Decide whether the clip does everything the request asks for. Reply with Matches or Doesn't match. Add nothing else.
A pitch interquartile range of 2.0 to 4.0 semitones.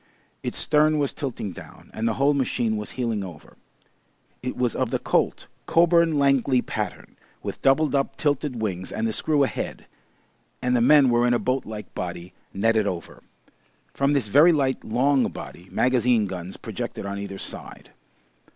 Doesn't match